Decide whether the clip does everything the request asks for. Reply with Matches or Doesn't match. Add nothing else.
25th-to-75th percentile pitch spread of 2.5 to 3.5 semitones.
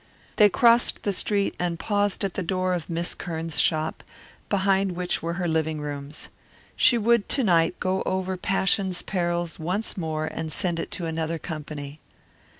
Matches